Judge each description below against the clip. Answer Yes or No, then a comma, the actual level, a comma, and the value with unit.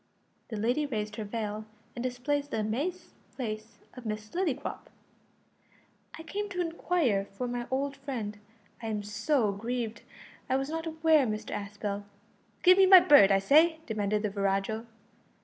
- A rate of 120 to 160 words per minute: Yes, average, 155 wpm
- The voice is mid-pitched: No, high, 240 Hz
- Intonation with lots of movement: Yes, wide, 5.8 semitones